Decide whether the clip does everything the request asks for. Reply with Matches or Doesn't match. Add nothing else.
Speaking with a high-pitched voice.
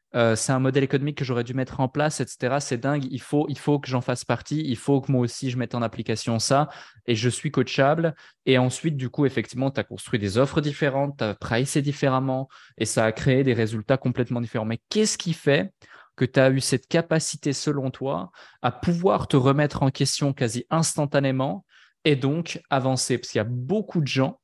Doesn't match